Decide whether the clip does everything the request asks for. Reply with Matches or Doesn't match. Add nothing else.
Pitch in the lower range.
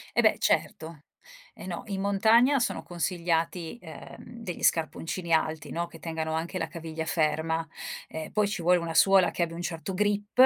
Doesn't match